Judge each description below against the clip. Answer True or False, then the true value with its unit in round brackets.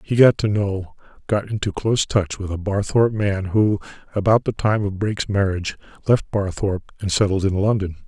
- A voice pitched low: True (100 Hz)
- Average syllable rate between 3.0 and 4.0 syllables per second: False (5.5 syllables/s)